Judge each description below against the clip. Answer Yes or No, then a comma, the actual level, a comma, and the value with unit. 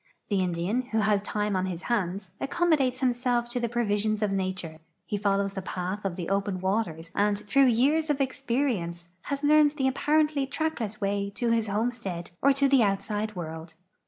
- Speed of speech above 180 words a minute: Yes, average, 190 wpm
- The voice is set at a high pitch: Yes, high, 210 Hz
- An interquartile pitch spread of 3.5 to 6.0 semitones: Yes, average, 5.2 semitones